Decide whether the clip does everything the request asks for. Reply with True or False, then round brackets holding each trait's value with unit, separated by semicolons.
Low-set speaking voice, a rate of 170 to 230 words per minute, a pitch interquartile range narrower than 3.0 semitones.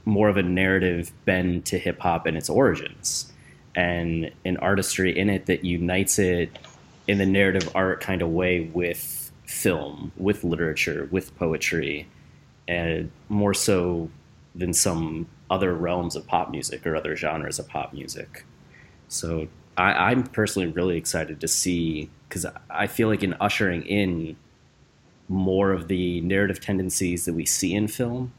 False (90 Hz; 155 wpm; 2.5 semitones)